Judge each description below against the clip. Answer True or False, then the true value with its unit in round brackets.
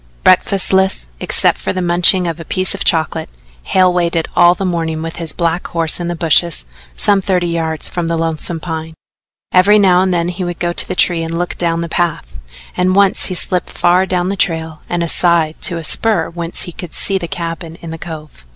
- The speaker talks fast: True (215 wpm)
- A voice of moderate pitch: True (175 Hz)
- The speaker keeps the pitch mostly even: True (1.9 semitones)